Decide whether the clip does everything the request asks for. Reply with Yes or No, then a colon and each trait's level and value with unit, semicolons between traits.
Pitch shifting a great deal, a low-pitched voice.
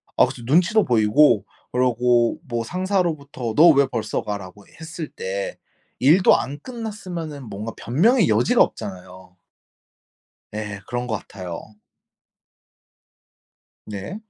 Yes: wide, 8.1 semitones; low, 125 Hz